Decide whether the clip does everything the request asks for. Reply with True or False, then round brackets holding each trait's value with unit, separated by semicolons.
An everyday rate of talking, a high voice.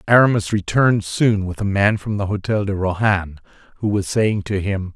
False (195 wpm; 100 Hz)